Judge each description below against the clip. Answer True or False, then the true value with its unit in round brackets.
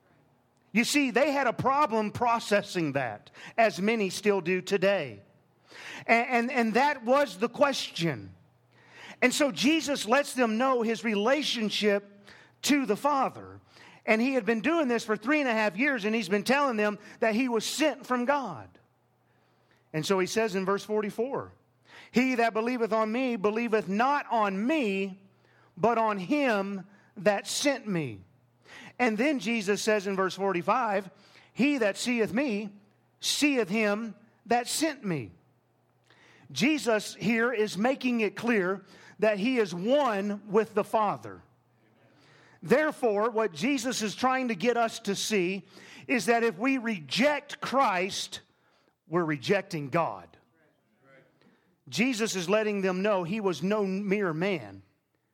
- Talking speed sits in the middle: True (145 wpm)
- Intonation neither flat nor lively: True (4.2 semitones)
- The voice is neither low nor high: False (215 Hz)